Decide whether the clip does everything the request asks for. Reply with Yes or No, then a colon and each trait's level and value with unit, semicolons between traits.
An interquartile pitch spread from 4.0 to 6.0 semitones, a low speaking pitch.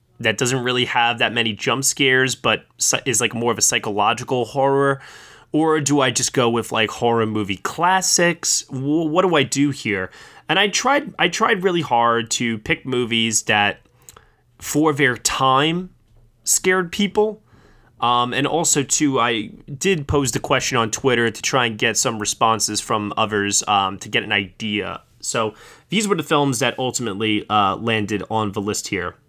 Yes: average, 4.5 semitones; low, 120 Hz